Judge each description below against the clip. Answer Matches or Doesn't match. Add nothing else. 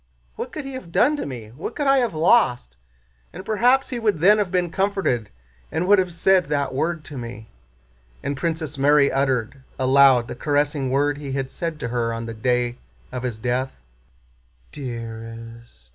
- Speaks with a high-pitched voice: Doesn't match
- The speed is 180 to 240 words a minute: Matches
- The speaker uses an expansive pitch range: Matches